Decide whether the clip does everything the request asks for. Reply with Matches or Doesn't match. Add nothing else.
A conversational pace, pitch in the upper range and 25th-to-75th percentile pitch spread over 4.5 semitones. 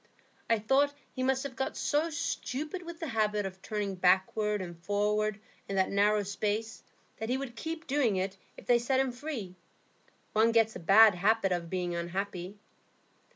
Matches